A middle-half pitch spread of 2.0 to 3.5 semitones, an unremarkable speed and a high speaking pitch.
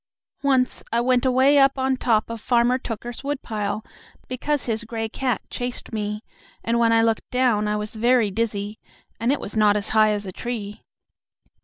Yes: average, 3.0 semitones; average, 180 wpm; high, 230 Hz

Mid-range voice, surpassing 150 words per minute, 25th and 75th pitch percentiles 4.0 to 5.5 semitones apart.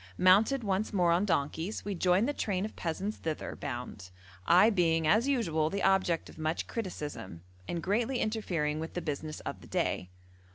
Yes: medium, 180 Hz; average, 175 wpm; average, 4.8 semitones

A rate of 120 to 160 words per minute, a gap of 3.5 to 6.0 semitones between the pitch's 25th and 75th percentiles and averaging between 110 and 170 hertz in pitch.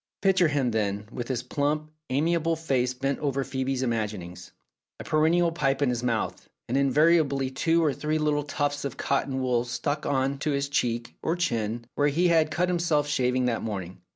No: average, 180 wpm; average, 3.8 semitones; medium, 140 Hz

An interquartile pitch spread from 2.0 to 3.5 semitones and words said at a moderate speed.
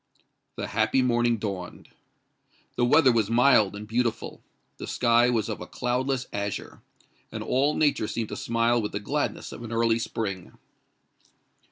Yes: narrow, 2.4 semitones; average, 155 wpm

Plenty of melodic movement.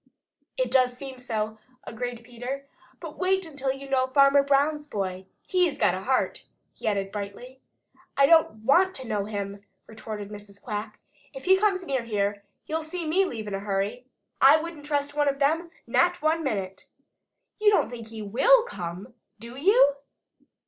Yes: wide, 6.6 semitones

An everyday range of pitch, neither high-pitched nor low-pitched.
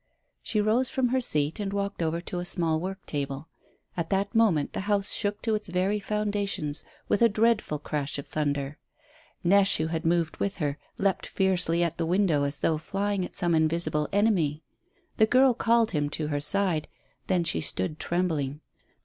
Yes: average, 4.8 semitones; medium, 175 Hz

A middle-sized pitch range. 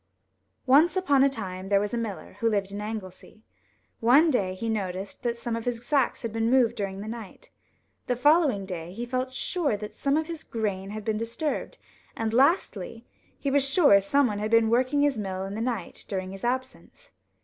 Yes: average, 4.6 semitones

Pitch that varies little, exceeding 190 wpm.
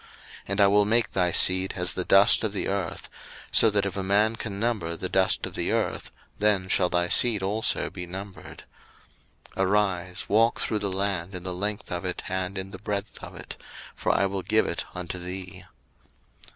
Yes: narrow, 2.1 semitones; fast, 205 wpm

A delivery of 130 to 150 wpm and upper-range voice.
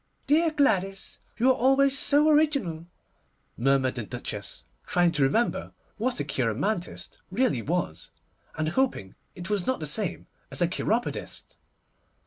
Yes: slow, 135 wpm; high, 195 Hz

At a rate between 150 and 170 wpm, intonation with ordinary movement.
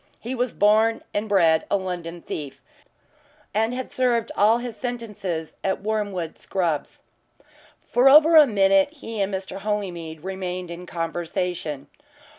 No: slow, 135 wpm; average, 4.6 semitones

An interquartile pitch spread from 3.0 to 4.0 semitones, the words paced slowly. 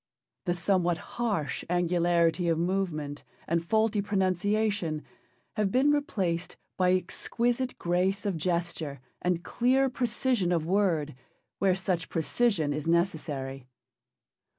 Yes: average, 3.7 semitones; slow, 110 wpm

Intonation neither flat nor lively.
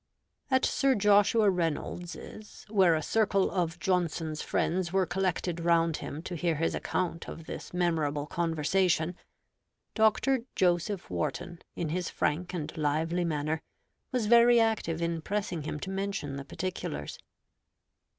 Yes: average, 3.2 semitones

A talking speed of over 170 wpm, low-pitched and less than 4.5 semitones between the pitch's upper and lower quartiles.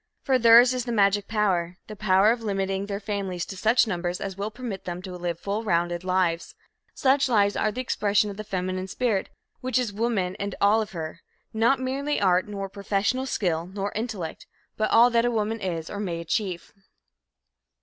No: average, 190 wpm; high, 200 Hz; average, 3.4 semitones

